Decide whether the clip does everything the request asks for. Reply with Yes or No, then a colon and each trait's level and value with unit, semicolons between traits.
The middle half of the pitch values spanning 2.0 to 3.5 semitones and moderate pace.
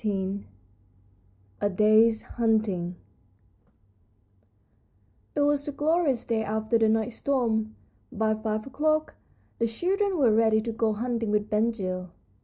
No: average, 2.7 semitones; slow, 125 wpm